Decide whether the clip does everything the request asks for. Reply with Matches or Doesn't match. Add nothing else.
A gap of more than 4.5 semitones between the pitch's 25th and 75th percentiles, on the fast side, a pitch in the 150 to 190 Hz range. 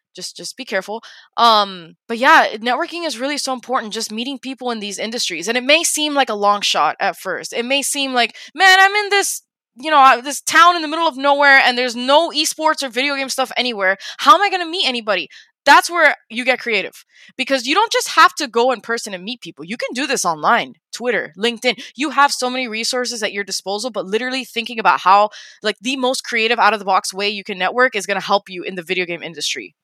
Doesn't match